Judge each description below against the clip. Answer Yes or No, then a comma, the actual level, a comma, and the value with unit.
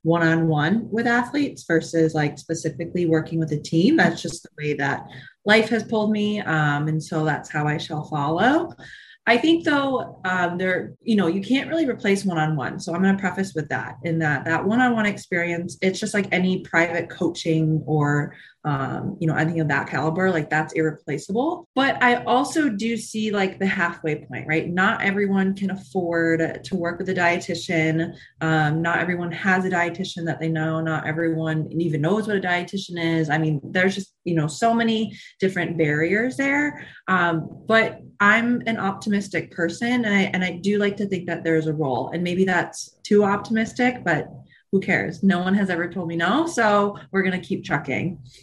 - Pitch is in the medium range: Yes, medium, 175 Hz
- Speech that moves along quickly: No, average, 190 wpm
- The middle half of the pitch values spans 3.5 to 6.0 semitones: Yes, average, 4.1 semitones